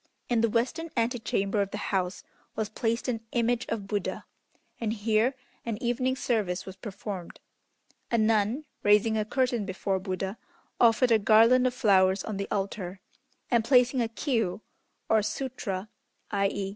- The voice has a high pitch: Yes, high, 220 Hz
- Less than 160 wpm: Yes, average, 150 wpm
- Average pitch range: Yes, average, 3.2 semitones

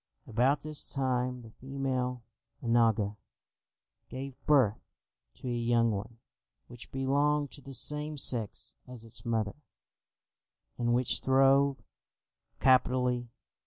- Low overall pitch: Yes, low, 125 Hz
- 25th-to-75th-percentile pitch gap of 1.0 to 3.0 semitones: Yes, narrow, 2.6 semitones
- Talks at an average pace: No, slow, 110 wpm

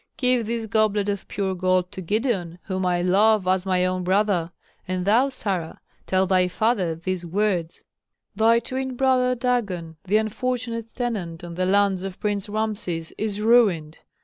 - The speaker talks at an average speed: Yes, average, 160 wpm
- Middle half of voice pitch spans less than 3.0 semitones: No, average, 3.5 semitones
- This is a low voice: No, high, 200 Hz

